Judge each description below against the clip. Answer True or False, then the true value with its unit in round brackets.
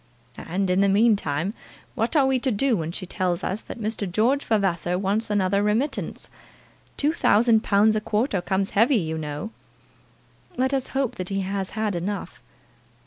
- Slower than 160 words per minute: False (170 wpm)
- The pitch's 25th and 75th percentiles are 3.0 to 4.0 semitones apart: True (3.6 semitones)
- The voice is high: True (205 Hz)